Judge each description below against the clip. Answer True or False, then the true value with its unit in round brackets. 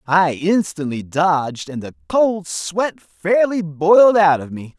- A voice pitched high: False (170 Hz)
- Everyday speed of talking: True (150 wpm)